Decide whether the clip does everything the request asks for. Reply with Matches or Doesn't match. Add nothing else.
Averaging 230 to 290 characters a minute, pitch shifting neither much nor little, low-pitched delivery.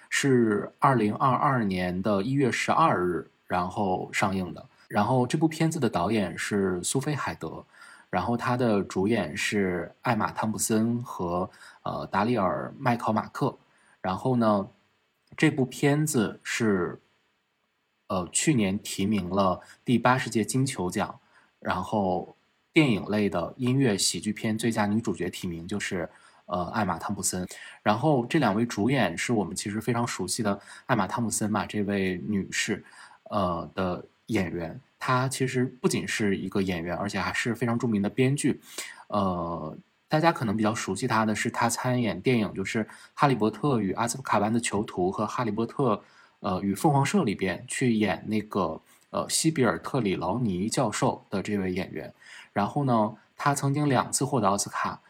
Matches